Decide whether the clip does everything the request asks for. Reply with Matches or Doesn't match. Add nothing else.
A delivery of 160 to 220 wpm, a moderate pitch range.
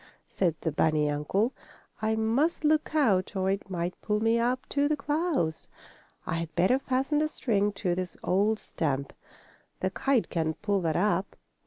Doesn't match